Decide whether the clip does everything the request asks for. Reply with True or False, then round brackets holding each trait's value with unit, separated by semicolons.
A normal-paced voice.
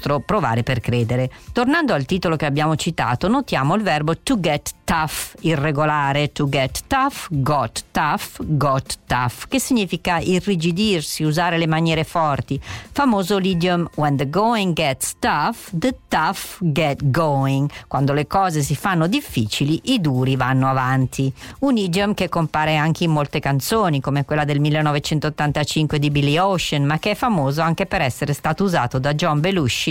True (155 wpm)